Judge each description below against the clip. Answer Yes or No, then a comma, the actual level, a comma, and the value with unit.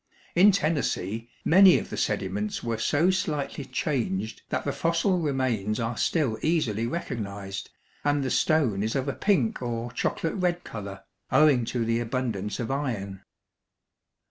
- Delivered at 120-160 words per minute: Yes, average, 145 wpm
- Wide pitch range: Yes, wide, 6.2 semitones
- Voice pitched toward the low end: Yes, low, 125 Hz